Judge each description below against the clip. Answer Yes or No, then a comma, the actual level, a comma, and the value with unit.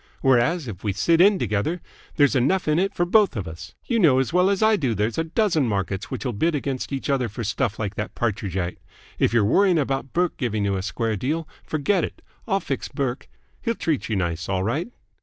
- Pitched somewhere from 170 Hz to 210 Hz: No, low, 130 Hz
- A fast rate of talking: Yes, fast, 225 wpm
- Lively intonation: Yes, wide, 8.1 semitones